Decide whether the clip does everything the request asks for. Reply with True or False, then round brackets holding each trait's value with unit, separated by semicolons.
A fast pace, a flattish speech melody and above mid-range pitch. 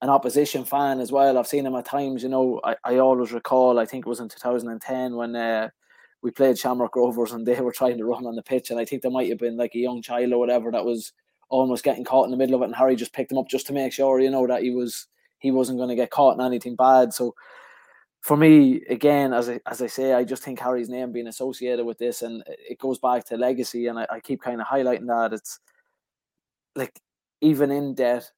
False (255 wpm; 1.6 semitones; 125 Hz)